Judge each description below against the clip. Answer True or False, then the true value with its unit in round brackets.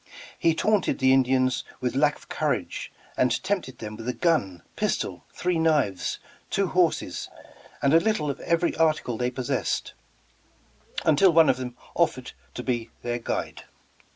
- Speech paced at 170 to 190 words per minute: False (155 wpm)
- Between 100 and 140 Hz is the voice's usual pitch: True (135 Hz)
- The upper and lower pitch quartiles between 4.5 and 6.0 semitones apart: True (5.2 semitones)